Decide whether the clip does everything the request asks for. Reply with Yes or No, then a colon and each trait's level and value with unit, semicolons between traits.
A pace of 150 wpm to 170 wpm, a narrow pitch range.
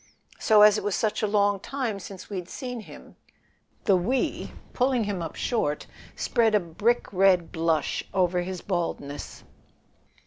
No: average, 160 wpm; average, 3.6 semitones